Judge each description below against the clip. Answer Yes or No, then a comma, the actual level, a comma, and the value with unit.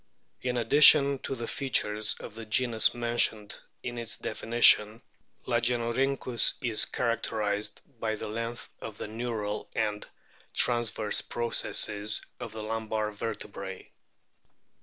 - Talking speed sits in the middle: No, slow, 115 wpm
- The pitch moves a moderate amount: No, narrow, 2.0 semitones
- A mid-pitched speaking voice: No, low, 115 Hz